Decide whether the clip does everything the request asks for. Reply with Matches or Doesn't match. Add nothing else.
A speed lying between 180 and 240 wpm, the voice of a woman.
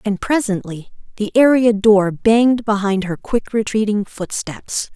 Doesn't match